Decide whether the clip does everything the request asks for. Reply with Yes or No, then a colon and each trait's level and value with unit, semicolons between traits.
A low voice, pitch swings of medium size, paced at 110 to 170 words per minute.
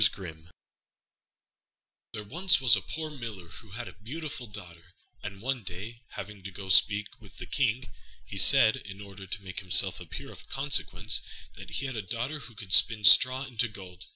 No: low, 105 Hz; average, 4.4 semitones; average, 185 wpm